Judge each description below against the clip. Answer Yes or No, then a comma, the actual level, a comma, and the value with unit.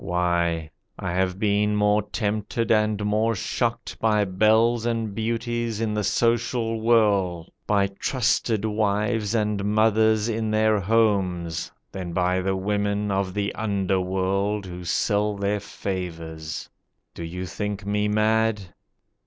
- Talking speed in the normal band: No, slow, 130 wpm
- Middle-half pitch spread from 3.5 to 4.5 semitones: No, narrow, 2.6 semitones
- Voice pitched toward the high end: No, low, 105 Hz